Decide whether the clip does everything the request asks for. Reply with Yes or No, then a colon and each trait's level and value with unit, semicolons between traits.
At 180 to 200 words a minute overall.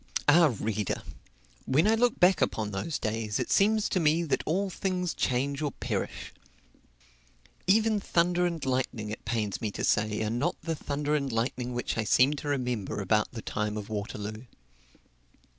No: average, 170 wpm